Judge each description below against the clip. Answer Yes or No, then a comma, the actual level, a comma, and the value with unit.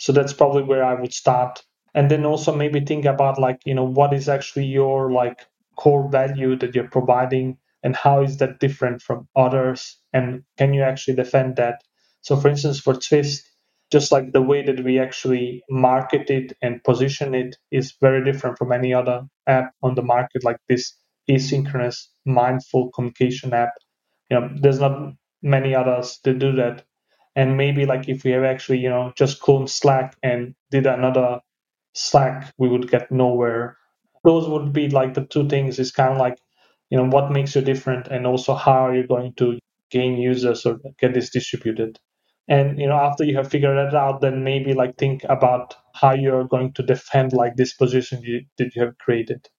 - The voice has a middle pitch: No, low, 130 Hz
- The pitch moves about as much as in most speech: No, narrow, 1.7 semitones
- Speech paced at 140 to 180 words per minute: No, average, 190 wpm